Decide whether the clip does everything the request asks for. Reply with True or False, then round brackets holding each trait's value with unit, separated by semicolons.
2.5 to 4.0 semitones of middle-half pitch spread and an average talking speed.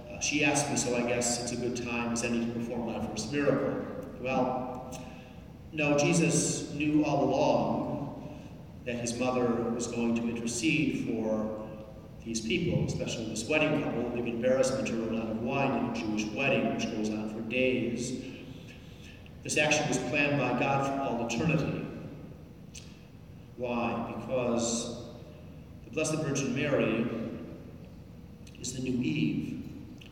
True (2.8 semitones; 145 wpm)